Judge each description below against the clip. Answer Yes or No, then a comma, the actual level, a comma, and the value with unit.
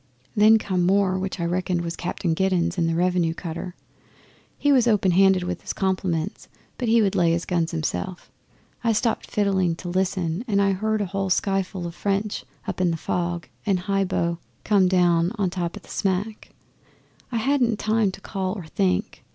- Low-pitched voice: No, medium, 185 Hz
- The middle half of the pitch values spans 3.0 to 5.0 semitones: No, narrow, 2.6 semitones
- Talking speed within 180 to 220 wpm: Yes, average, 190 wpm